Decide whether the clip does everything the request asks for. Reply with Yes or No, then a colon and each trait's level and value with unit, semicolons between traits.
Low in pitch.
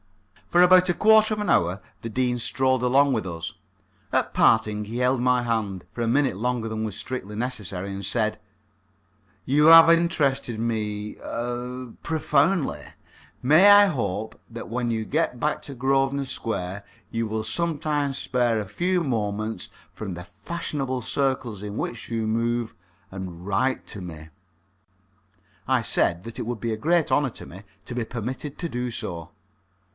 Yes: low, 120 Hz